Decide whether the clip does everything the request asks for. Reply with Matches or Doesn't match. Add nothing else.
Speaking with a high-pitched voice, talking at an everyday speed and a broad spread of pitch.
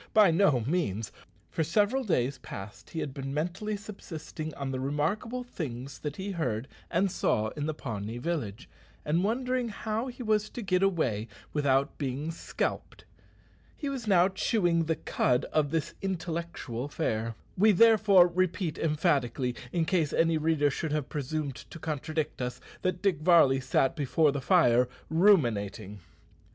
Doesn't match